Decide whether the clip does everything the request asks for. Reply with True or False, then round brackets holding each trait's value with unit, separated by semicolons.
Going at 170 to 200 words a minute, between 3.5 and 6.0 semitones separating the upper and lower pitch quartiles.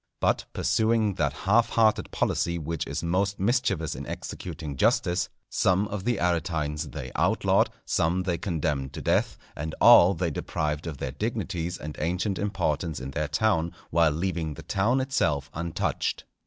False (155 wpm; 4.2 semitones)